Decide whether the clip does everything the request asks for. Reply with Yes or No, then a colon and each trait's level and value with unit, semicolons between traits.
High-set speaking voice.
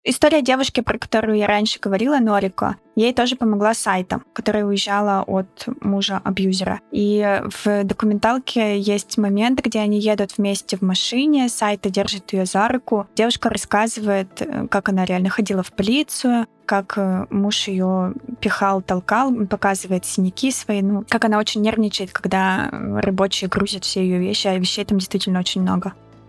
Yes: high, 205 Hz